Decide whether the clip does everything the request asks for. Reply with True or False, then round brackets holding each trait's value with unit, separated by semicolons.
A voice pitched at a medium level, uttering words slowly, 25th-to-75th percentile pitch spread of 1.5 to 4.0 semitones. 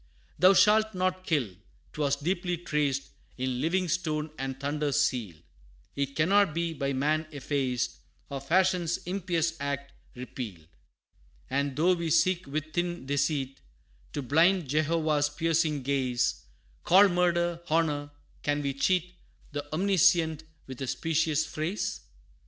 True (155 Hz; 130 wpm; 3.6 semitones)